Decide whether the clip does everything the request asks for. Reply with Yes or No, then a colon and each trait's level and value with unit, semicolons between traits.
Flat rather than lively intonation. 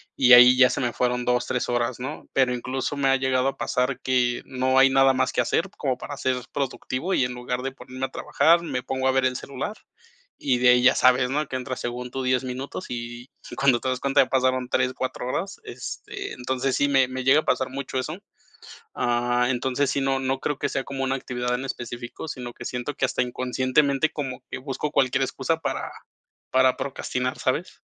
Yes: narrow, 1.3 semitones